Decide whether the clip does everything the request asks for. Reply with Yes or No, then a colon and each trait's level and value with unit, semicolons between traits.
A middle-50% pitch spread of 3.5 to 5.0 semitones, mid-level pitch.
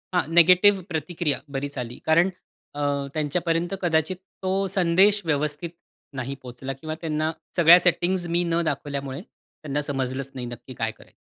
Yes: average, 4.1 semitones; medium, 155 Hz